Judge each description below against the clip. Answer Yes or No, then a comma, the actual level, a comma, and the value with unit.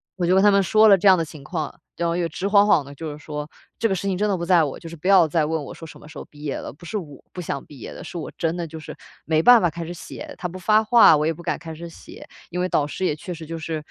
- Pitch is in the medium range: Yes, medium, 170 Hz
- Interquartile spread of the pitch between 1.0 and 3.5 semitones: Yes, average, 3.2 semitones